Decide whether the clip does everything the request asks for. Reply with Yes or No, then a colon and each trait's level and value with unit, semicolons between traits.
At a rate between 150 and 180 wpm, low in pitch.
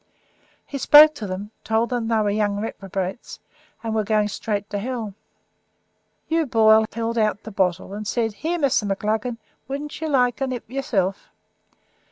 No: average, 170 wpm; high, 220 Hz